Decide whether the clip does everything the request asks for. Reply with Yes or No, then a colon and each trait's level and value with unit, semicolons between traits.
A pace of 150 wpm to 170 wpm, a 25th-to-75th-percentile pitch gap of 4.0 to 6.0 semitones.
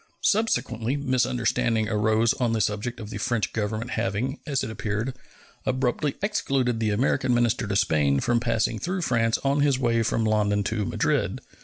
No: average, 165 wpm; average, 3.2 semitones